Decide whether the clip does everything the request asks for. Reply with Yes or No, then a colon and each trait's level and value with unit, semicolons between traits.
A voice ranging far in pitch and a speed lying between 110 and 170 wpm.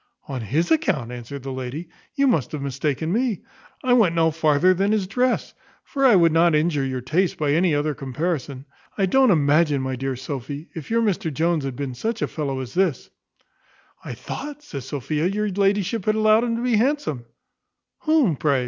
No: wide, 7.2 semitones; average, 195 wpm